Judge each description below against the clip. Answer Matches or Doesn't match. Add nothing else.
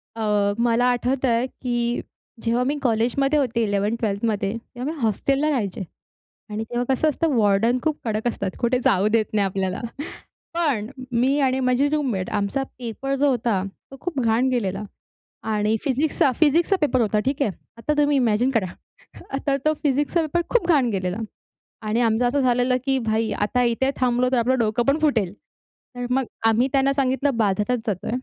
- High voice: Matches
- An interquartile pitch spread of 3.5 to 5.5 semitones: Matches